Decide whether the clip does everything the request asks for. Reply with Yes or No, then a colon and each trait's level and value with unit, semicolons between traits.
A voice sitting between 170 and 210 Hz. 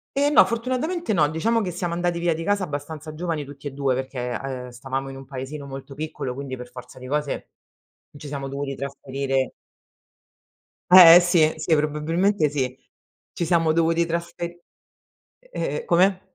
No: medium, 150 Hz